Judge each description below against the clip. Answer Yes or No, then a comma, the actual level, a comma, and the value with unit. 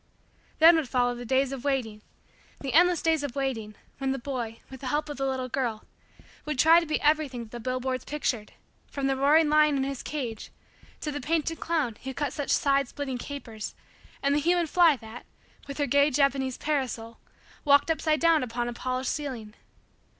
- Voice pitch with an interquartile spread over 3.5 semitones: No, average, 3.2 semitones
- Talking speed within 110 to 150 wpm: No, average, 195 wpm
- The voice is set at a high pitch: Yes, very high, 275 Hz